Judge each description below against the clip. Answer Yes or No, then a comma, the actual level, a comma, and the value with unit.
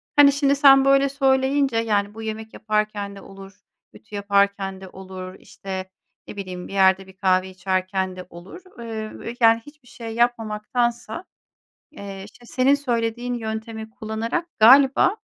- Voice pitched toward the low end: No, high, 220 Hz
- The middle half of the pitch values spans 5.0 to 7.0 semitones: No, average, 4.2 semitones